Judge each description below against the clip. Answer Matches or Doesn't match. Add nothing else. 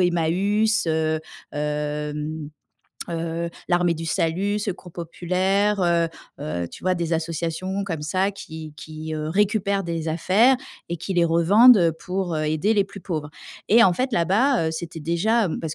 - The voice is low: Doesn't match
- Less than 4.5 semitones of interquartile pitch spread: Matches